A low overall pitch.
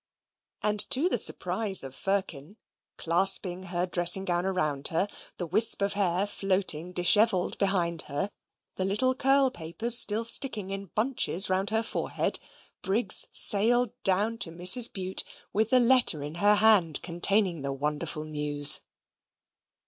No: high, 190 Hz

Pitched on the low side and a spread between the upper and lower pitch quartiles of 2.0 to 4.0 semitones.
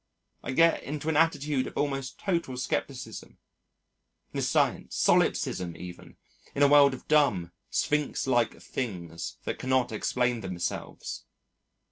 No: low, 130 Hz; average, 4.8 semitones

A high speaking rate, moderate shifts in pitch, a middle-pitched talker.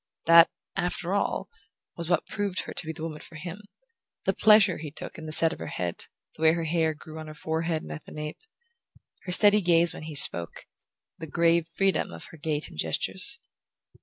No: fast, 210 wpm; narrow, 2.3 semitones; medium, 165 Hz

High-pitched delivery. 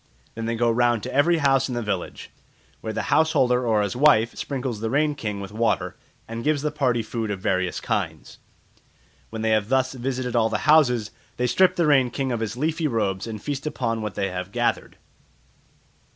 No: low, 120 Hz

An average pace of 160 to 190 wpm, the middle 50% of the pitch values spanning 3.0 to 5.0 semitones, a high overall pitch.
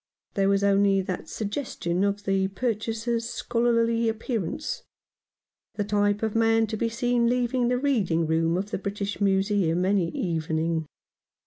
No: average, 145 wpm; average, 3.3 semitones; high, 205 Hz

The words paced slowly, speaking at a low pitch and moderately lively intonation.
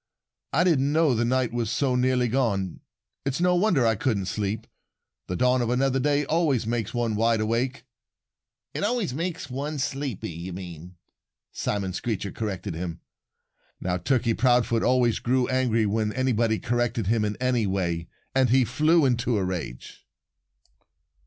No: average, 155 wpm; low, 120 Hz; average, 4.0 semitones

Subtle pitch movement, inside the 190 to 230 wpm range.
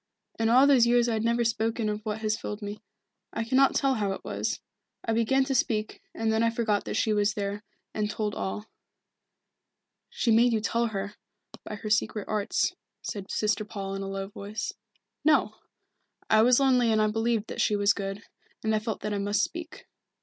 Yes: narrow, 1.9 semitones; average, 200 wpm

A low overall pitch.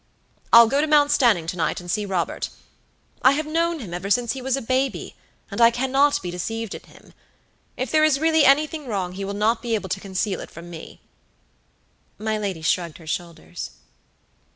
No: high, 225 Hz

